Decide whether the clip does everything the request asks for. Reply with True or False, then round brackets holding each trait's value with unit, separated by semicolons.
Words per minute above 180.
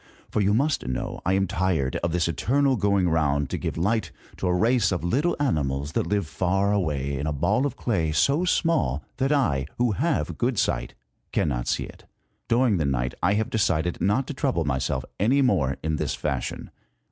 True (195 wpm)